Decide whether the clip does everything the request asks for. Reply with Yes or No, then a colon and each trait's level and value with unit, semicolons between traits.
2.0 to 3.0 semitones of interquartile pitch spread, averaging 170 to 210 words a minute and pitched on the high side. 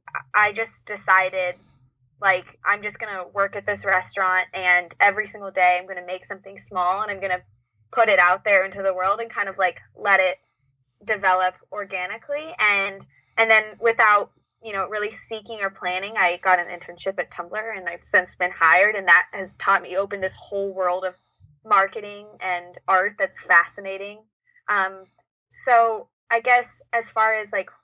Yes: narrow, 2.5 semitones; average, 180 wpm; high, 195 Hz